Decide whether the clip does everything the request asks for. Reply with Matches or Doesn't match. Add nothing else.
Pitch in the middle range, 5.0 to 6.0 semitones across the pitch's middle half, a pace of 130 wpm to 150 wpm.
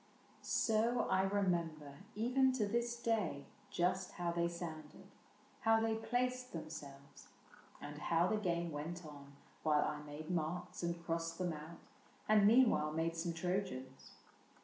Matches